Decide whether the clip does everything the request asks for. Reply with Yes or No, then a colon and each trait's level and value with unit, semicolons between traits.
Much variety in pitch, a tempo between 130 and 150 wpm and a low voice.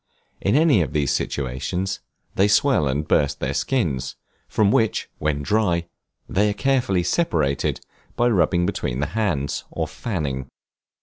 Yes: wide, 6.9 semitones; average, 140 wpm; very low, 85 Hz